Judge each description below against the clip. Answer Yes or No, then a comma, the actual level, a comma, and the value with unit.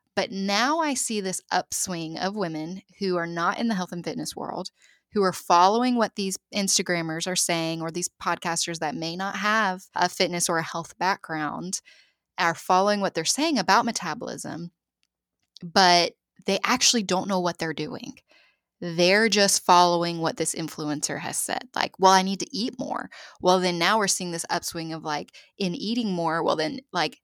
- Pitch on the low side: No, medium, 180 Hz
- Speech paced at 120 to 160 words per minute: No, average, 185 wpm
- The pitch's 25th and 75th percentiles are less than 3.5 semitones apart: Yes, average, 2.9 semitones